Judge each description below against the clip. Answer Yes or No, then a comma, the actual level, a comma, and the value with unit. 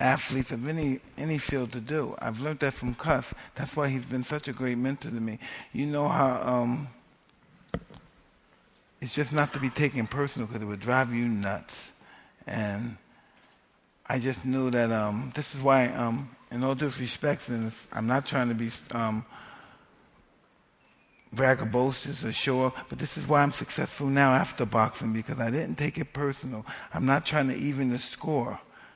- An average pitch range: Yes, average, 3.2 semitones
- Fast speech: No, average, 175 wpm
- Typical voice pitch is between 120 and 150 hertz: Yes, low, 130 Hz